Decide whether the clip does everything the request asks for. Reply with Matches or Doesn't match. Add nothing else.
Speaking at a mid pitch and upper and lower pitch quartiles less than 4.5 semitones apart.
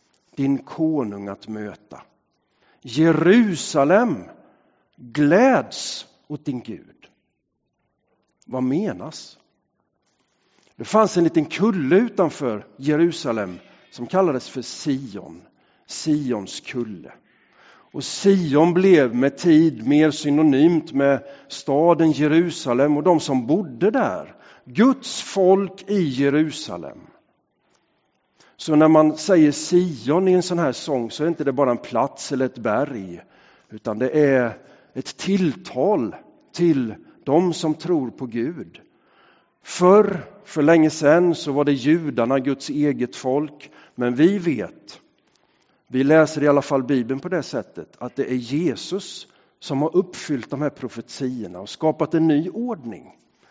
Matches